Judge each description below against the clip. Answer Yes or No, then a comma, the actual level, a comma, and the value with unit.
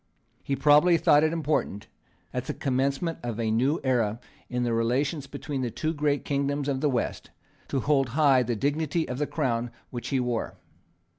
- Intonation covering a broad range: No, average, 3.3 semitones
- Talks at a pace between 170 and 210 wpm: Yes, average, 180 wpm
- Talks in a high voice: No, low, 135 Hz